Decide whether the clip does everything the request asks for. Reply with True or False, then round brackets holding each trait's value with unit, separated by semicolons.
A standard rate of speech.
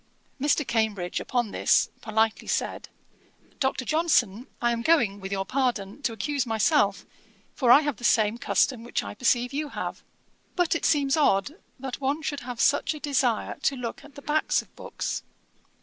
True (175 wpm)